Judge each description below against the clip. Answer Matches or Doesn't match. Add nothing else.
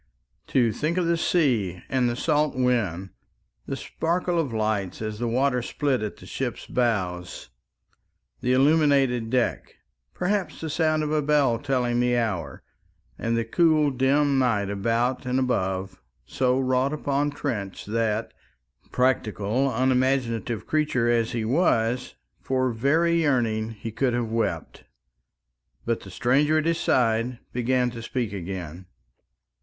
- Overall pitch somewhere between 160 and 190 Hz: Doesn't match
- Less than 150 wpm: Matches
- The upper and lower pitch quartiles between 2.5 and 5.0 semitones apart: Matches